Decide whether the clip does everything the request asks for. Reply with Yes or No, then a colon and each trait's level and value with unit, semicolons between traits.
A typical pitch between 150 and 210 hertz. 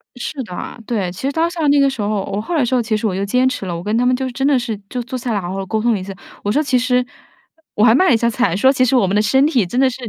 No: high, 240 Hz